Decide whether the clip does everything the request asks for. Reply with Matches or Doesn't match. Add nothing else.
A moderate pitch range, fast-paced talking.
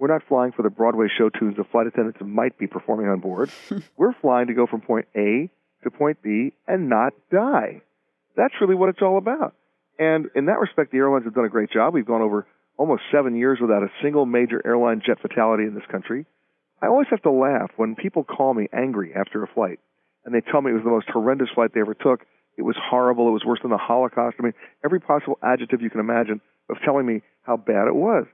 Matches